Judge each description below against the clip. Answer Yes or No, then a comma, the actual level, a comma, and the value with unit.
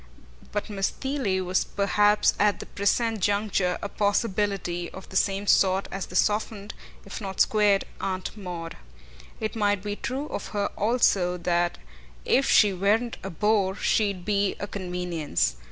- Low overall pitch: No, high, 200 Hz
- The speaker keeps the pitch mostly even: Yes, narrow, 2.1 semitones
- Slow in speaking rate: No, average, 155 wpm